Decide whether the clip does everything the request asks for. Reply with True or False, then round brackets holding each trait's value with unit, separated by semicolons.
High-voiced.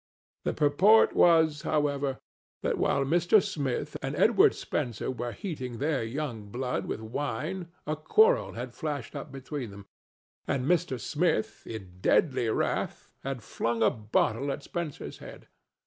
False (140 Hz)